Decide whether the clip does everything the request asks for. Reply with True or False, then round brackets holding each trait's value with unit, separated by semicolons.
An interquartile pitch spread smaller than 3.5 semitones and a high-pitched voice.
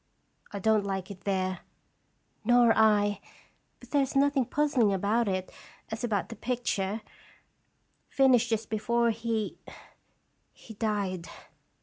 True (3.0 semitones; 220 Hz)